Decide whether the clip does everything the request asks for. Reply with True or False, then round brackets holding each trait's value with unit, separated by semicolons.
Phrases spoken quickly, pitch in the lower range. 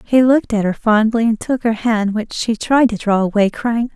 False (245 wpm; 225 Hz)